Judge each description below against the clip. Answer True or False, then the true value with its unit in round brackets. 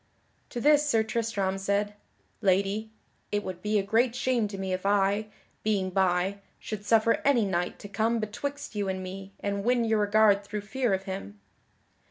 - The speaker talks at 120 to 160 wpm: False (180 wpm)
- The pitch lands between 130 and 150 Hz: False (205 Hz)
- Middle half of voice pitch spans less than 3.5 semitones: True (2.4 semitones)